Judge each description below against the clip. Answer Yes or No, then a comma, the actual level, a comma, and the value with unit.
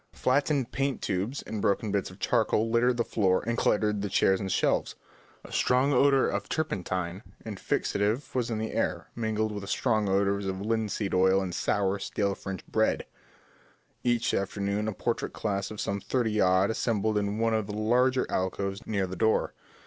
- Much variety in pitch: No, average, 2.9 semitones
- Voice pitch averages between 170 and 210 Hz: No, low, 105 Hz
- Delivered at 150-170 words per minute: No, average, 180 wpm